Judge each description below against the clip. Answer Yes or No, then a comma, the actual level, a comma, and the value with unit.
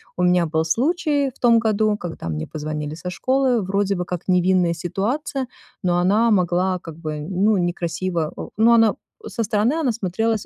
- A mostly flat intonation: No, average, 4.6 semitones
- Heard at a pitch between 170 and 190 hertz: Yes, medium, 185 Hz